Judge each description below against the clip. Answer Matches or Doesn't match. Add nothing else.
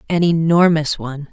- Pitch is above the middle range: Doesn't match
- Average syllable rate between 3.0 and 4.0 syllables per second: Doesn't match